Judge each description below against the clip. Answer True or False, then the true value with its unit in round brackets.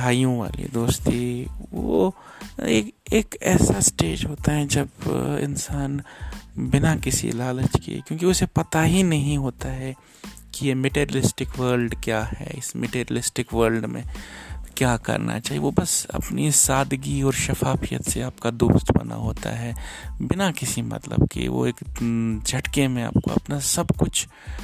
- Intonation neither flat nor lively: True (3.4 semitones)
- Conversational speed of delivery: True (145 wpm)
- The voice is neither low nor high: False (125 Hz)